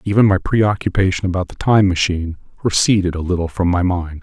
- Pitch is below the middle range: Yes, very low, 95 Hz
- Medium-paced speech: Yes, average, 185 wpm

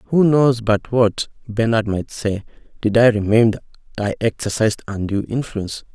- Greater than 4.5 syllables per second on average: Yes, 5.0 syllables/s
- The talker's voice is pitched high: No, low, 110 Hz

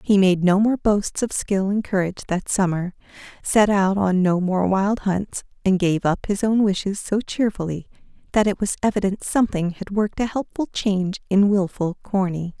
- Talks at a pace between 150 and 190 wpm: Yes, average, 185 wpm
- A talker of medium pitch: No, high, 195 Hz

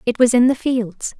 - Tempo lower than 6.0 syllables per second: Yes, 4.7 syllables/s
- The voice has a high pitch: Yes, high, 245 Hz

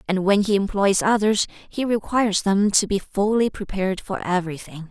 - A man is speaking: No, female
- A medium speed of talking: Yes, average, 170 wpm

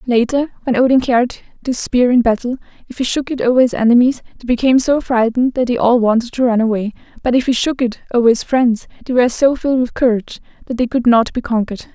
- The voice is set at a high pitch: Yes, high, 245 Hz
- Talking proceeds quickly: Yes, fast, 230 wpm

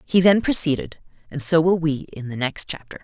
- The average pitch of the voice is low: No, medium, 155 Hz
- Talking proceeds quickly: Yes, fast, 220 wpm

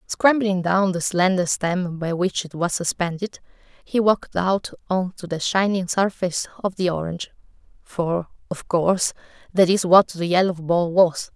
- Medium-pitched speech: Yes, medium, 180 Hz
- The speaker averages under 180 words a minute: Yes, average, 165 wpm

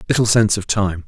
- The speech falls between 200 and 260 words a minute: Yes, fast, 225 wpm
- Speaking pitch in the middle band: No, low, 100 Hz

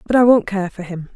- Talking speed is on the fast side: Yes, fast, 310 wpm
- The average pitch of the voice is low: No, high, 200 Hz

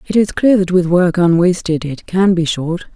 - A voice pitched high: No, medium, 175 Hz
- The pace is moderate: No, fast, 225 wpm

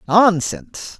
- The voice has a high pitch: No, medium, 175 Hz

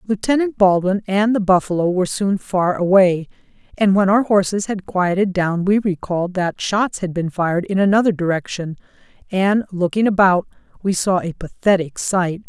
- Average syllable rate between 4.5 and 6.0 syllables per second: Yes, 5.0 syllables/s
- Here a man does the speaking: No, female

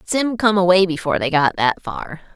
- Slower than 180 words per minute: No, fast, 205 wpm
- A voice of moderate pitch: Yes, medium, 180 Hz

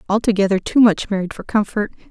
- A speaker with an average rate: Yes, average, 170 wpm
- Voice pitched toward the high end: Yes, high, 205 Hz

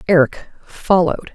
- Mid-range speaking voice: Yes, medium, 175 Hz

